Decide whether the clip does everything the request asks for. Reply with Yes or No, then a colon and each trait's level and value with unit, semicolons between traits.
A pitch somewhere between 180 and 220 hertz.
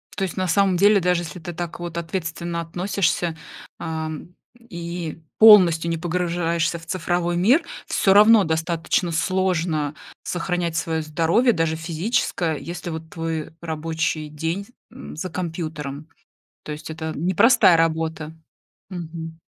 No: medium, 170 Hz